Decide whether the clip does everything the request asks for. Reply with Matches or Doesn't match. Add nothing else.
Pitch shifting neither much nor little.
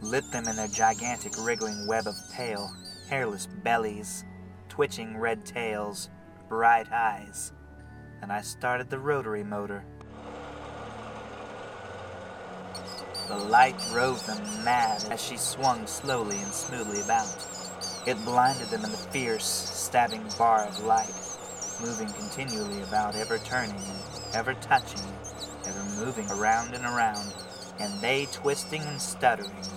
Matches